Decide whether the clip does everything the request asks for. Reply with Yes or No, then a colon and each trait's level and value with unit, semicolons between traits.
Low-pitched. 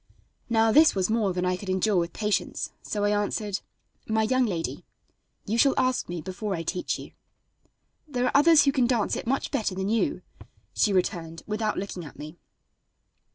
No: high, 210 Hz